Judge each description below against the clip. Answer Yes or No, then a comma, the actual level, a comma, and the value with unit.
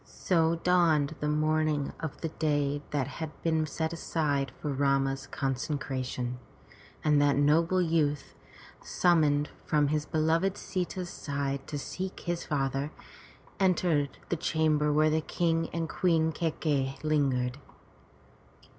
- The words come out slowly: Yes, slow, 130 wpm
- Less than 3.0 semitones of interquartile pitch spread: Yes, narrow, 2.5 semitones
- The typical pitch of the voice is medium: Yes, medium, 155 Hz